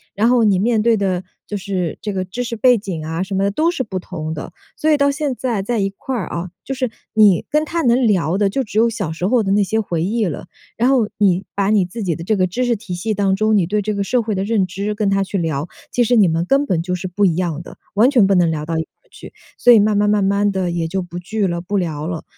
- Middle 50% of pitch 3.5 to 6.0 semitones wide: Yes, average, 3.9 semitones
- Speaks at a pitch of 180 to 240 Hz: Yes, high, 200 Hz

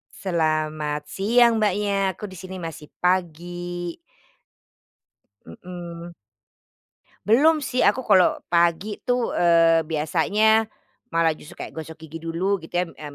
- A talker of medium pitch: Yes, medium, 175 Hz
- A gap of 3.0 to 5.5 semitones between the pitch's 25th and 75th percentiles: Yes, average, 3.6 semitones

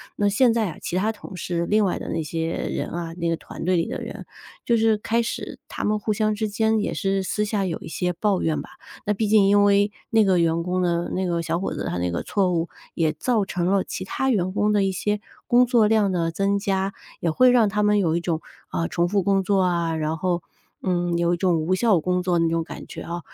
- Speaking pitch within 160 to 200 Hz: Yes, high, 190 Hz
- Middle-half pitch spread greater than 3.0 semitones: Yes, average, 3.5 semitones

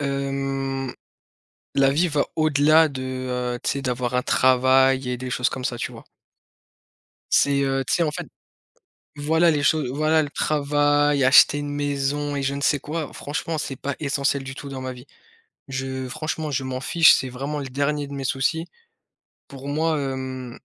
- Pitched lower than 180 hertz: Yes, medium, 140 Hz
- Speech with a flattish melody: Yes, narrow, 1.9 semitones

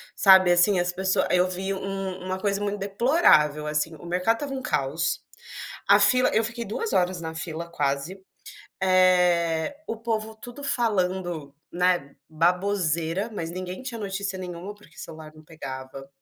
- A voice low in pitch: No, medium, 185 Hz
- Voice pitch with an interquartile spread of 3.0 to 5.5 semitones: Yes, average, 3.6 semitones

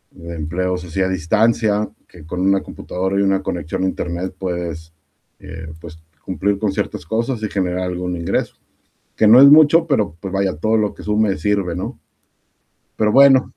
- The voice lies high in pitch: No, very low, 95 Hz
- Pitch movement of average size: Yes, average, 3.4 semitones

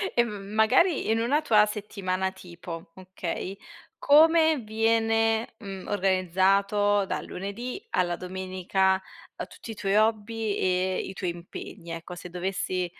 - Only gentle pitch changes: No, average, 3.2 semitones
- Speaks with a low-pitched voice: No, high, 195 Hz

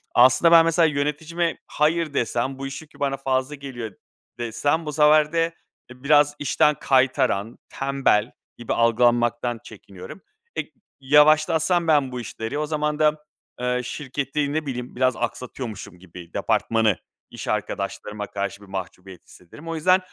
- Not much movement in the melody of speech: No, average, 4.2 semitones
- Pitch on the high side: No, low, 135 Hz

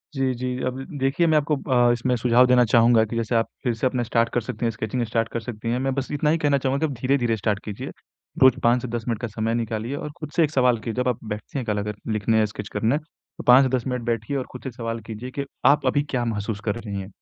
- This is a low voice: Yes, low, 120 Hz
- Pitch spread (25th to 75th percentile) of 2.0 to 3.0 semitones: Yes, narrow, 2.6 semitones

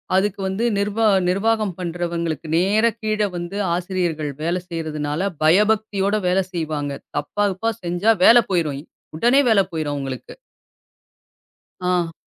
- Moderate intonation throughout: Yes, average, 4.2 semitones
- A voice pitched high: No, medium, 180 Hz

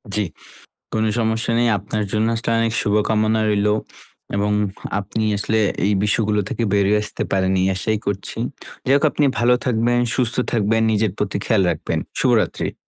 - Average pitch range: No, narrow, 1.8 semitones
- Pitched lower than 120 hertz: Yes, low, 110 Hz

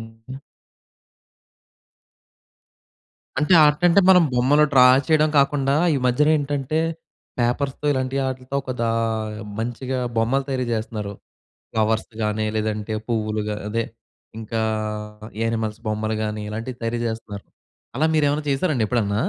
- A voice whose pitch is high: No, low, 120 Hz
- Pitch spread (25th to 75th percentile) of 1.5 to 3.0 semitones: No, average, 4.1 semitones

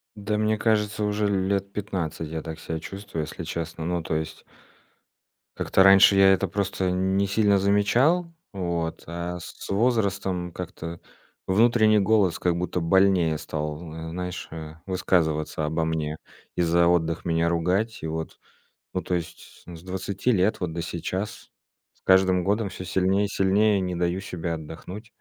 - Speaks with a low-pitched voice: Yes, very low, 90 Hz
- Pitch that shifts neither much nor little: Yes, average, 3.2 semitones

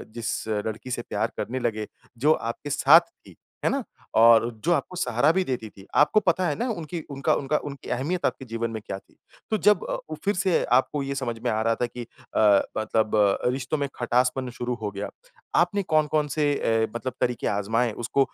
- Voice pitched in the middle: No, low, 130 Hz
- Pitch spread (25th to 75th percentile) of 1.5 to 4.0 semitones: No, average, 5.2 semitones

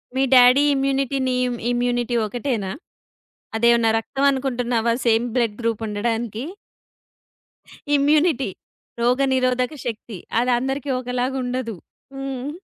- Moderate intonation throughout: No, narrow, 2.3 semitones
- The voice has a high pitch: Yes, high, 245 Hz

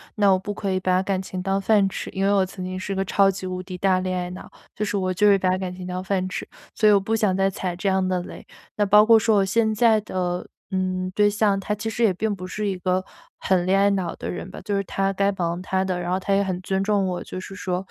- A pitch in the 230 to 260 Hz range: No, high, 190 Hz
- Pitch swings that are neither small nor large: No, narrow, 1.6 semitones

